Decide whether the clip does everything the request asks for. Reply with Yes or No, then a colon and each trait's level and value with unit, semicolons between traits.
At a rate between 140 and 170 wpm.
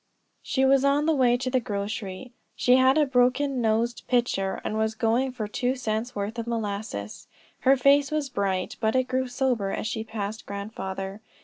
No: average, 185 wpm